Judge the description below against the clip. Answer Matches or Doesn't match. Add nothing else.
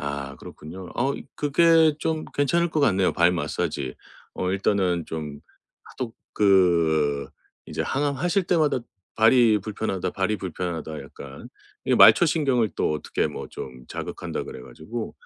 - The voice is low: Matches